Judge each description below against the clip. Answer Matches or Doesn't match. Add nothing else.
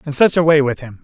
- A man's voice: Matches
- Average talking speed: Doesn't match